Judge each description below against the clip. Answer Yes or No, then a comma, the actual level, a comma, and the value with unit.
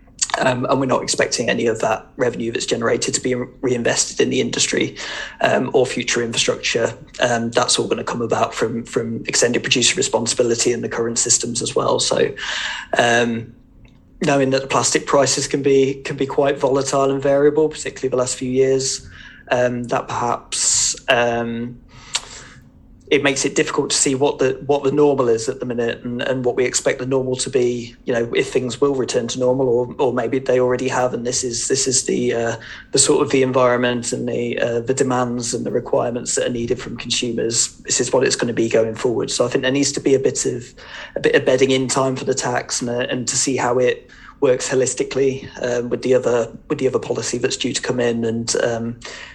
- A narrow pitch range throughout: Yes, narrow, 2.0 semitones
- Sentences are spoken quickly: Yes, fast, 215 wpm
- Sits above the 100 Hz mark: Yes, low, 125 Hz